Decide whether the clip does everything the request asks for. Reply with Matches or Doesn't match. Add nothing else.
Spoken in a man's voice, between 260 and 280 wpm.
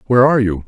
Matches